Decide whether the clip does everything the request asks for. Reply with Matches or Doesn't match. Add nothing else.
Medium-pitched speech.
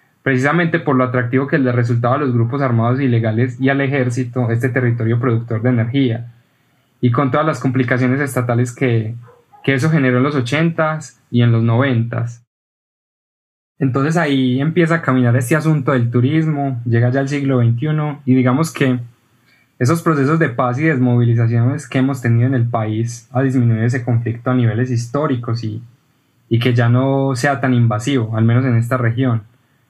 Doesn't match